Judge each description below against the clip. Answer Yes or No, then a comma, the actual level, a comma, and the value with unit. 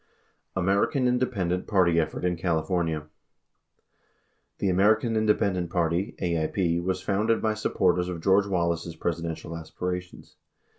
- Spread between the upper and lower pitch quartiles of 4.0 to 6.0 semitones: No, average, 2.9 semitones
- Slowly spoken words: Yes, slow, 110 wpm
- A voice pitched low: Yes, very low, 90 Hz